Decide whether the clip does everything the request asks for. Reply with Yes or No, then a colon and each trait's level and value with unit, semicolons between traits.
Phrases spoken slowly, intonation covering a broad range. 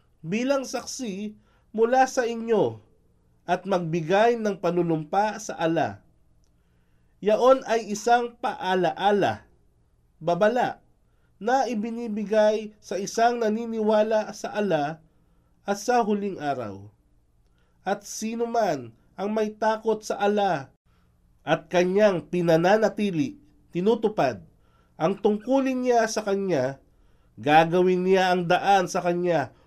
Yes: slow, 100 wpm; wide, 5.9 semitones